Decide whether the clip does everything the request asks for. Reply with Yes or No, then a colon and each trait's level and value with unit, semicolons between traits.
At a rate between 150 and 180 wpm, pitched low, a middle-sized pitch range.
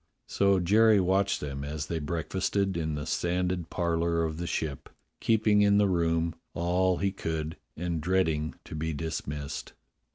Yes: average, 155 wpm; very low, 85 Hz; average, 3.2 semitones